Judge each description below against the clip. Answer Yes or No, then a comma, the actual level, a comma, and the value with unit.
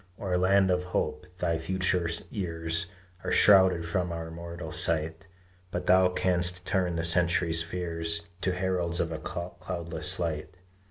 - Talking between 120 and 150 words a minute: Yes, average, 145 wpm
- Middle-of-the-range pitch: No, very low, 85 Hz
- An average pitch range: No, narrow, 1.8 semitones